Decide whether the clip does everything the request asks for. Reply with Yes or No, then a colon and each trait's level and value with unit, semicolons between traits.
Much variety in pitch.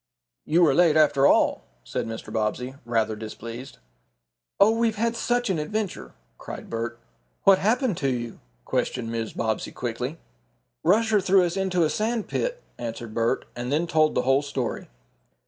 Yes: wide, 8.9 semitones